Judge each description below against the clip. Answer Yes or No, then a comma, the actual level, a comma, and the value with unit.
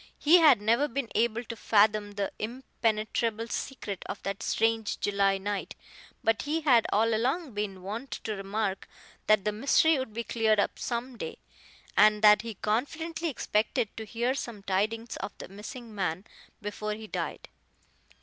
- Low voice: No, high, 220 Hz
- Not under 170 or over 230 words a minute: No, average, 160 wpm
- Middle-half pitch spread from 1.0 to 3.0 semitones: Yes, narrow, 2.5 semitones